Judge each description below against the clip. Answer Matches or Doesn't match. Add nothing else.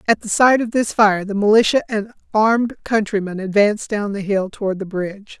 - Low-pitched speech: Doesn't match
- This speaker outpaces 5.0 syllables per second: Matches